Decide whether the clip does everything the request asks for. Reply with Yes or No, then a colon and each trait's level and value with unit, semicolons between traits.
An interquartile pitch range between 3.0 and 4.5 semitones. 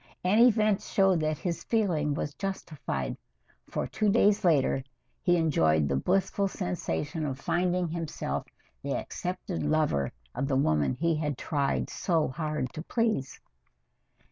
No: average, 5.3 semitones